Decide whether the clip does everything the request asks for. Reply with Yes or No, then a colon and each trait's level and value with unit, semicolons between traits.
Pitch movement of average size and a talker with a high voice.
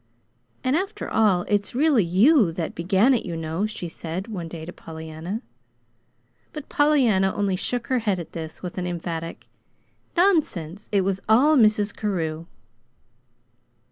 No: wide, 5.8 semitones; high, 195 Hz